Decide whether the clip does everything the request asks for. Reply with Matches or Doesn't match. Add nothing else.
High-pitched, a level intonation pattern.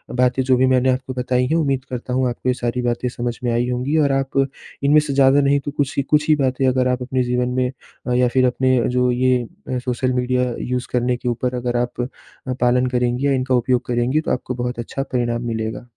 Doesn't match